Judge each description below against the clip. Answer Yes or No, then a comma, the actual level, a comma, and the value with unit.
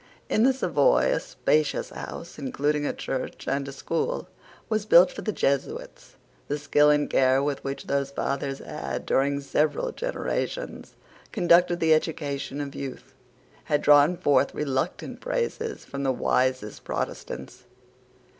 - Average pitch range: Yes, average, 3.9 semitones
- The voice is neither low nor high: Yes, medium, 145 Hz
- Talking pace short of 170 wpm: Yes, average, 140 wpm